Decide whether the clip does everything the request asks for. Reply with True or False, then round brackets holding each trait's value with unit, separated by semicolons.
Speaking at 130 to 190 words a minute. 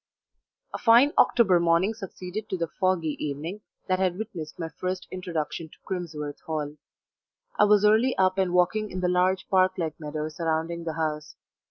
True (170 wpm)